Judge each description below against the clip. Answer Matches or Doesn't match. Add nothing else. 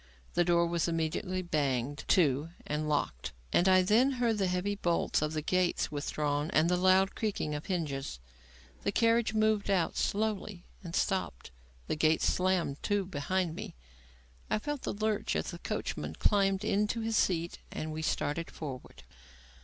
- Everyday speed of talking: Matches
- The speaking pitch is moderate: Matches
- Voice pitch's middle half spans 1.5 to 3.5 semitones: Doesn't match